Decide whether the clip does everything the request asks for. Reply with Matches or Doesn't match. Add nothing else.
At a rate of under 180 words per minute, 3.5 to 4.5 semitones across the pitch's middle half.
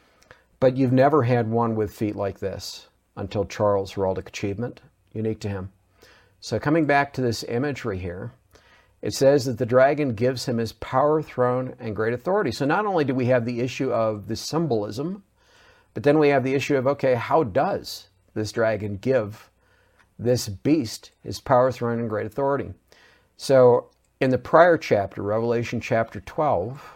Matches